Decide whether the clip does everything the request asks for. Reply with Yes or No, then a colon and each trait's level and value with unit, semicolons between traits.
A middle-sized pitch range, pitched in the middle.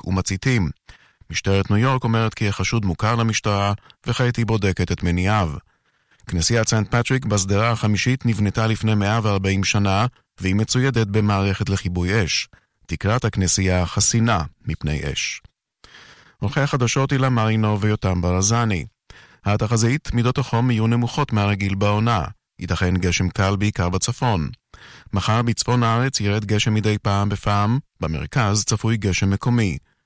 No: average, 3.3 semitones; low, 105 Hz